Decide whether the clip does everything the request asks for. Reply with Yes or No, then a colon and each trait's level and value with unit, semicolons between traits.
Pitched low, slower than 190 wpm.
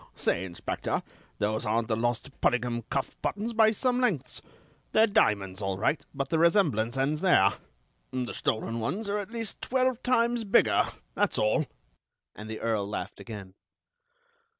Yes: low, 125 Hz; average, 150 wpm